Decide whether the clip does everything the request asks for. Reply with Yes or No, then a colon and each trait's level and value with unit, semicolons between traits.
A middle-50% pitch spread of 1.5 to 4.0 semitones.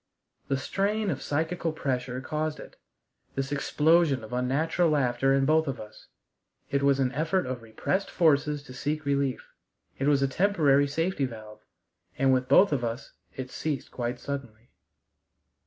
Yes: average, 3.4 semitones